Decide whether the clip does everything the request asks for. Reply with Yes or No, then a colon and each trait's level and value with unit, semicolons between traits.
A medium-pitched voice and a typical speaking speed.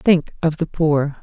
Yes: medium, 155 Hz; average, 195 wpm